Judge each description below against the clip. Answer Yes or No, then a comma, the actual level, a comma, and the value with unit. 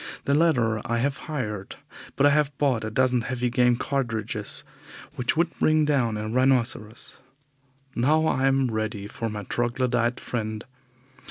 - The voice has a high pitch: No, low, 125 Hz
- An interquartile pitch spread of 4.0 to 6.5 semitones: No, average, 3.6 semitones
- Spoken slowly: No, average, 150 wpm